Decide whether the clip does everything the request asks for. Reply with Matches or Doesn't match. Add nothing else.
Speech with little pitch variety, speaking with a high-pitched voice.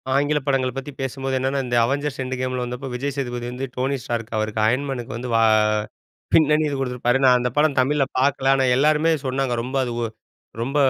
Doesn't match